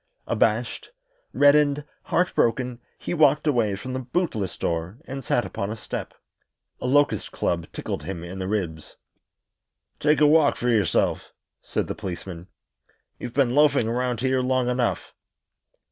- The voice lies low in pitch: Yes, low, 125 Hz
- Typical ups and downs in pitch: No, wide, 6.2 semitones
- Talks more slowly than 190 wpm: Yes, average, 145 wpm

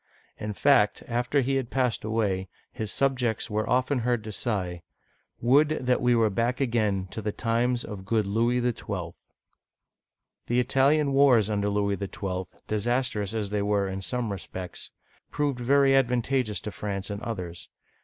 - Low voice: Yes, low, 115 Hz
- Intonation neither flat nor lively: Yes, average, 3.5 semitones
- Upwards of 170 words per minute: No, average, 160 wpm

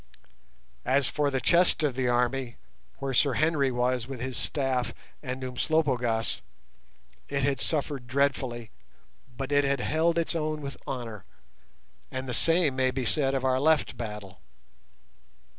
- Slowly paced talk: No, average, 145 wpm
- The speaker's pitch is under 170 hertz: Yes, low, 135 Hz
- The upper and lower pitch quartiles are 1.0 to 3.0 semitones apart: Yes, narrow, 2.6 semitones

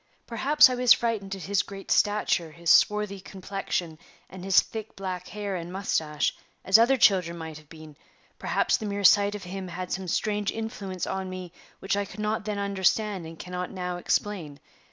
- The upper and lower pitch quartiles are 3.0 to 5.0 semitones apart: No, narrow, 2.6 semitones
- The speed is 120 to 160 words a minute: No, average, 185 wpm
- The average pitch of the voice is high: Yes, high, 195 Hz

